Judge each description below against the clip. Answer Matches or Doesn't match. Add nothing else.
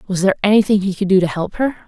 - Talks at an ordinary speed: Doesn't match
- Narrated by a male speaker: Doesn't match